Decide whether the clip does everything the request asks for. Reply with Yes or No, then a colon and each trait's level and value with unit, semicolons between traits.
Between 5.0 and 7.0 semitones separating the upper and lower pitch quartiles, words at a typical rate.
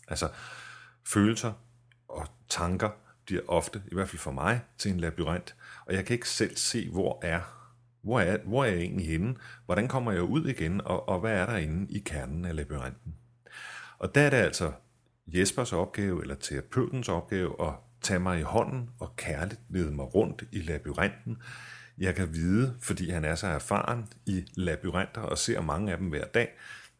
Yes: average, 5.3 semitones; average, 185 wpm